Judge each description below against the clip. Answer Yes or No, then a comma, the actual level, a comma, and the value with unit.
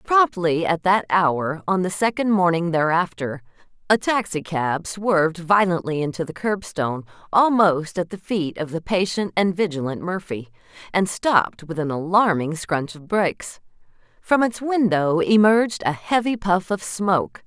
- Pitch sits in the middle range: Yes, medium, 180 Hz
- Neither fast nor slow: Yes, average, 150 wpm